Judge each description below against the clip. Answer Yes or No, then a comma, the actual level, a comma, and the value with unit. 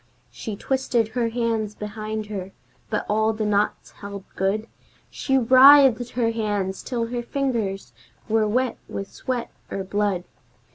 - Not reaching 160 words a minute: Yes, average, 140 wpm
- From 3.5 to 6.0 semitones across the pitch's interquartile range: No, average, 2.8 semitones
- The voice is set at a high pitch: Yes, high, 220 Hz